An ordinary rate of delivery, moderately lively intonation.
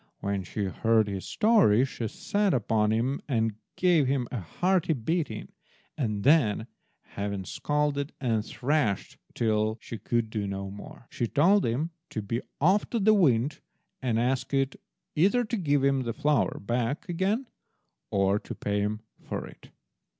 No: average, 155 wpm; wide, 6.1 semitones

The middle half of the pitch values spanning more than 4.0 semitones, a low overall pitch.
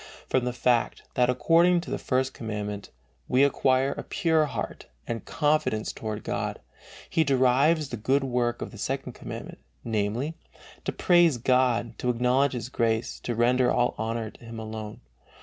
No: average, 3.0 semitones; low, 125 Hz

